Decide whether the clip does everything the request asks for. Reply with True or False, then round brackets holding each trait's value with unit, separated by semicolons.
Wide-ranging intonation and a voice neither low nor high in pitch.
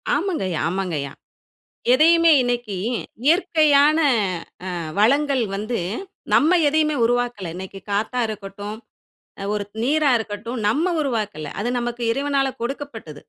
False (6.0 semitones; 245 Hz)